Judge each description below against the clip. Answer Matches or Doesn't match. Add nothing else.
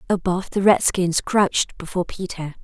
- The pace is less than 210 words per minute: Matches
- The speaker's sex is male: Doesn't match